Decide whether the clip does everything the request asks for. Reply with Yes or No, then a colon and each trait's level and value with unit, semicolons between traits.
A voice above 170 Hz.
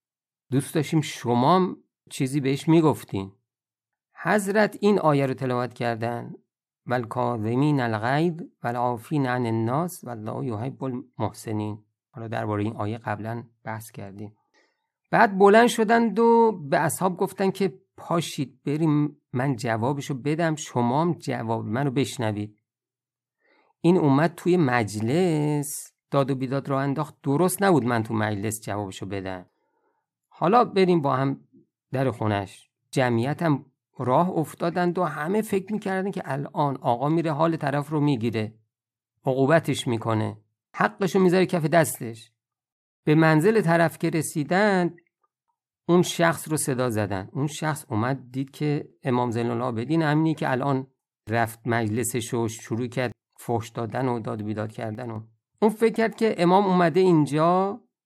No: medium, 140 Hz